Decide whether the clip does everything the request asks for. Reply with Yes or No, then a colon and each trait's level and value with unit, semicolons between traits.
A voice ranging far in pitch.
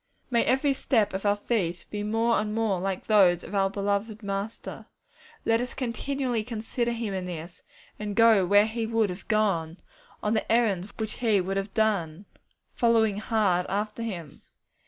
No: average, 2.7 semitones